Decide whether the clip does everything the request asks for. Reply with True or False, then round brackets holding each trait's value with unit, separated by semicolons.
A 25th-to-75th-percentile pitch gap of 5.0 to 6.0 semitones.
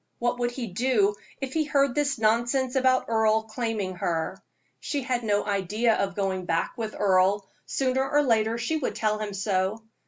False (4.2 semitones)